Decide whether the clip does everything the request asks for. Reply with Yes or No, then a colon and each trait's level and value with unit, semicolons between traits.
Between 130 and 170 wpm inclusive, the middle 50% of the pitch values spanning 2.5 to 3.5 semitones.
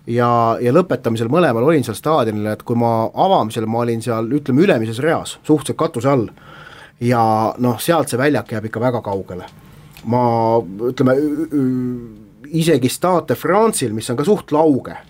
No: average, 160 wpm; average, 4.7 semitones